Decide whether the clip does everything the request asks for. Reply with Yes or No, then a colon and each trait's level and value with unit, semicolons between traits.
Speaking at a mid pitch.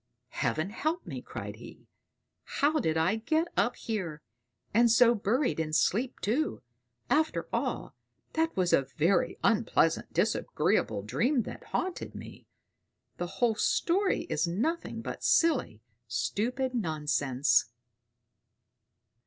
No: high, 220 Hz